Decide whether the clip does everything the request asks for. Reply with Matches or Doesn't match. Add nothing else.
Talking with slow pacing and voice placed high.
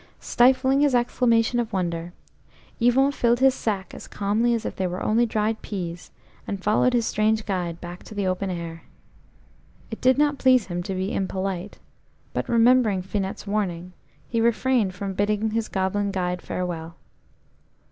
Doesn't match